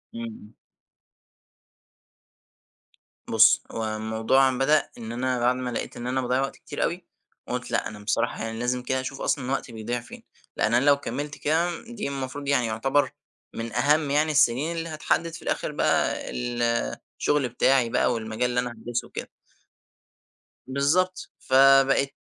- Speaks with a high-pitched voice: No, low, 130 Hz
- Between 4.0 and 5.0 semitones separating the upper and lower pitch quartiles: No, average, 3.1 semitones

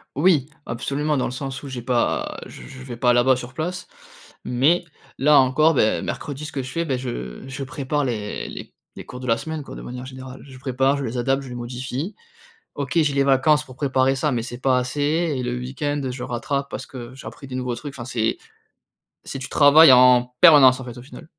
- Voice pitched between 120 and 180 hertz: Yes, low, 130 Hz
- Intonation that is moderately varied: No, narrow, 2.3 semitones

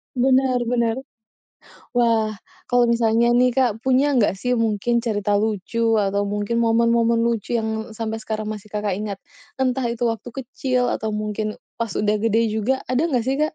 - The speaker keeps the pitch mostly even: Yes, narrow, 2.2 semitones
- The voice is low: No, high, 230 Hz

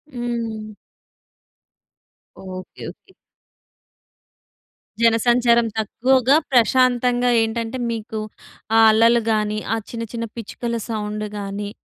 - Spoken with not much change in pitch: Yes, narrow, 1.9 semitones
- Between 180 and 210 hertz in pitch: No, high, 230 Hz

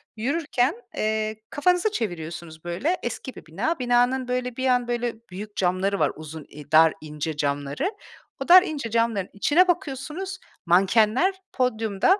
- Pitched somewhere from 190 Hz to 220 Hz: No, high, 230 Hz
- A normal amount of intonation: No, wide, 7.2 semitones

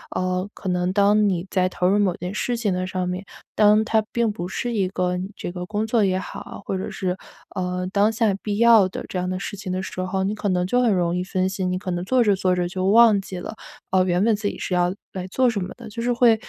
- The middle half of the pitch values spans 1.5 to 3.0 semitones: Yes, average, 2.7 semitones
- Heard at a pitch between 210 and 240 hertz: No, high, 190 Hz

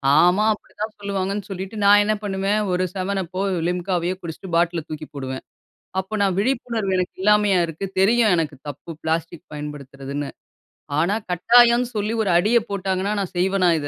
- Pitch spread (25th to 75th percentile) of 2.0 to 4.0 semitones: Yes, average, 3.6 semitones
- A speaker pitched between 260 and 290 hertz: No, high, 190 Hz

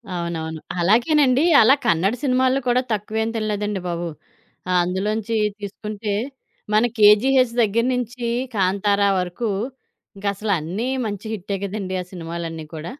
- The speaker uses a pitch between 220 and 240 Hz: No, high, 205 Hz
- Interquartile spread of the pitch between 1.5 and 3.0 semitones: No, average, 4.0 semitones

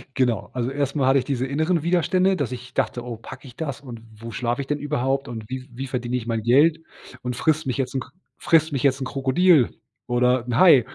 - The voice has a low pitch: Yes, low, 130 Hz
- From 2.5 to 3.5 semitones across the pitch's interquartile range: Yes, average, 2.9 semitones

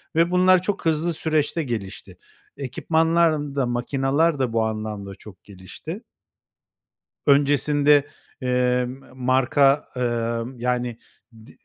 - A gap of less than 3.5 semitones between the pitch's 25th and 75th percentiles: No, average, 4.3 semitones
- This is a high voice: No, low, 135 Hz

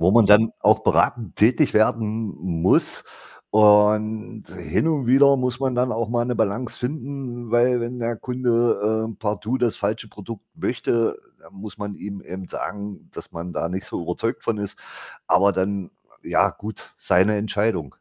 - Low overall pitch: Yes, low, 110 Hz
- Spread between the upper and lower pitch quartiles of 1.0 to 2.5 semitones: No, average, 2.9 semitones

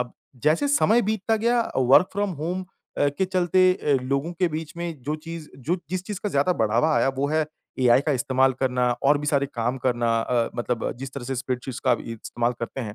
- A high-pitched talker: No, medium, 140 Hz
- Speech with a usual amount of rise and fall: No, wide, 5.8 semitones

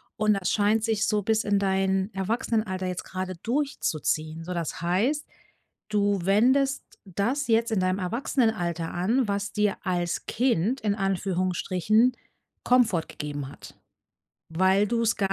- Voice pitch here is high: Yes, high, 200 Hz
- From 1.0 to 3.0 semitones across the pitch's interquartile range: No, average, 3.4 semitones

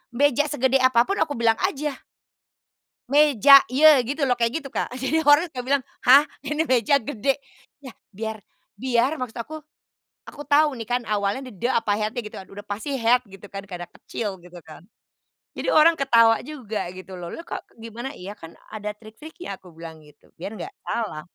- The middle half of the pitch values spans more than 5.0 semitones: Yes, wide, 5.5 semitones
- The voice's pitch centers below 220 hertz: No, high, 240 Hz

